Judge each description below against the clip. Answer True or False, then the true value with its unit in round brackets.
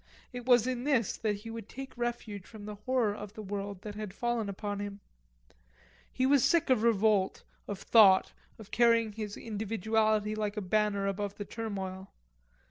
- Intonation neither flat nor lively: False (2.2 semitones)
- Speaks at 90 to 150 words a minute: False (175 wpm)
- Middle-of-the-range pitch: False (215 Hz)